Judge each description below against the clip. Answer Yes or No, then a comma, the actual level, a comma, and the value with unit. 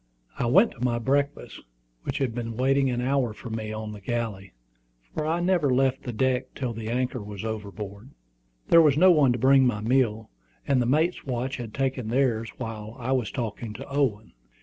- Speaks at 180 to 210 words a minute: Yes, average, 195 wpm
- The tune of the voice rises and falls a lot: No, average, 3.5 semitones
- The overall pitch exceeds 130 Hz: No, low, 125 Hz